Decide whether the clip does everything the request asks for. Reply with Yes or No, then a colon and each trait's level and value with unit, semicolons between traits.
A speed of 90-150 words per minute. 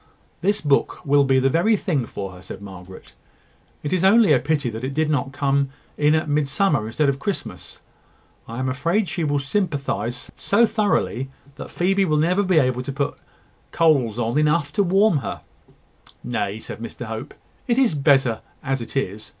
No: average, 180 wpm